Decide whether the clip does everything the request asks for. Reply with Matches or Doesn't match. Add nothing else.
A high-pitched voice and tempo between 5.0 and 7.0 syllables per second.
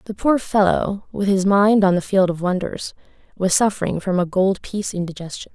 Matches